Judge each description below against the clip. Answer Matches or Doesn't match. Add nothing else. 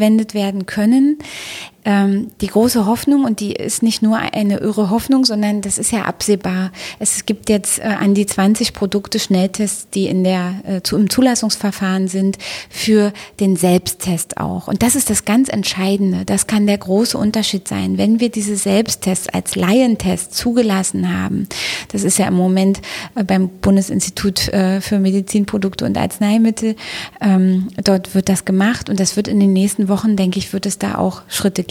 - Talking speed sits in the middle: Matches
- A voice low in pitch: Doesn't match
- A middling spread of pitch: Doesn't match